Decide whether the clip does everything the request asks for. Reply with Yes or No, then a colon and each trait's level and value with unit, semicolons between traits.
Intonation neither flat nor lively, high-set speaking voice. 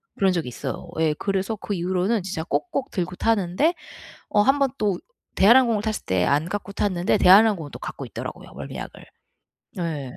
Yes: average, 3.8 semitones; high, 195 Hz